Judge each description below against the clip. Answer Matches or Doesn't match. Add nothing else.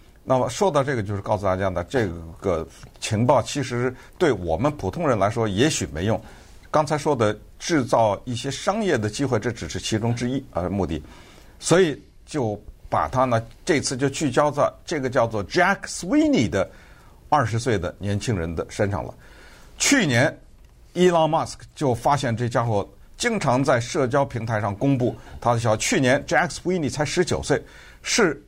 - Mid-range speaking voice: Doesn't match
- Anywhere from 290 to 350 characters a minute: Matches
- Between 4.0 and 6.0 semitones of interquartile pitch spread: Matches